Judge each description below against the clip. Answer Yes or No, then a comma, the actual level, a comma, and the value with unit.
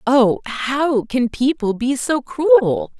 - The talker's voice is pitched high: Yes, high, 245 Hz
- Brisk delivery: No, average, 140 wpm